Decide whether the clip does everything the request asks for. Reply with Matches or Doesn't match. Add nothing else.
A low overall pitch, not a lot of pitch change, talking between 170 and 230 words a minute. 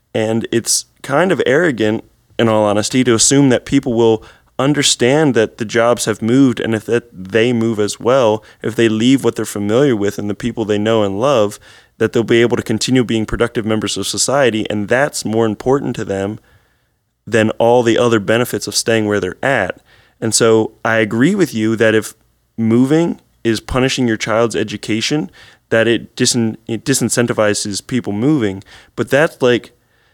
Matches